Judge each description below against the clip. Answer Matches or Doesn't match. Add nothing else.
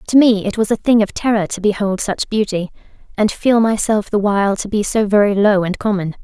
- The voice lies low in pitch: Doesn't match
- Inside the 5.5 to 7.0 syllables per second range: Matches